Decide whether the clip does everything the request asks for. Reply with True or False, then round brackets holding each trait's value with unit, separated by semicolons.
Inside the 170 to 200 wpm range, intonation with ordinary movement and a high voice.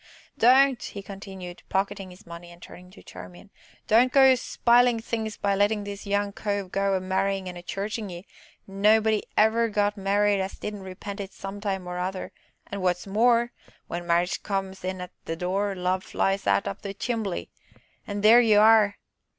False (175 wpm; 2.3 semitones; 200 Hz)